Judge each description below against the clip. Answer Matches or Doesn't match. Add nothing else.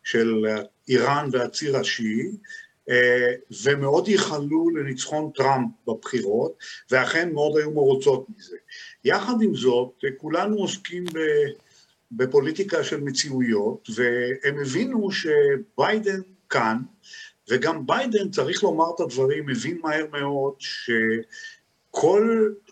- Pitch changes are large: Matches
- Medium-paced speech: Doesn't match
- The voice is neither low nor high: Matches